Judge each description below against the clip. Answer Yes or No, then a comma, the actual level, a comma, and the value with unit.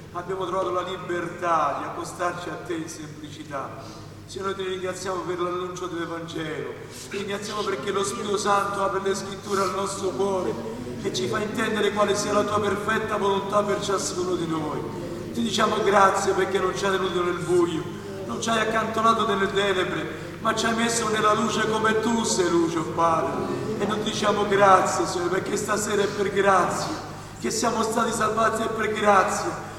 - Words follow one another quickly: Yes, fast, 180 wpm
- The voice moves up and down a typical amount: Yes, average, 3.0 semitones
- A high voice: Yes, high, 195 Hz